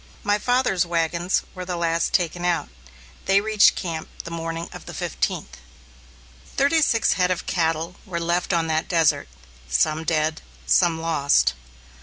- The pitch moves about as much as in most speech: No, narrow, 2.1 semitones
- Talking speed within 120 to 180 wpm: Yes, average, 150 wpm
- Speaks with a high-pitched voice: No, medium, 170 Hz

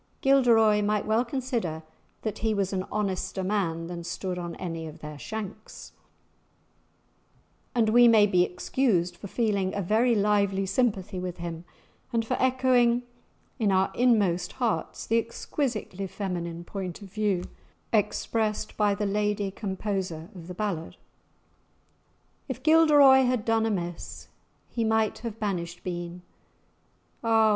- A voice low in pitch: No, high, 205 Hz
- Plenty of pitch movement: No, average, 3.9 semitones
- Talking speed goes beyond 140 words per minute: No, slow, 135 wpm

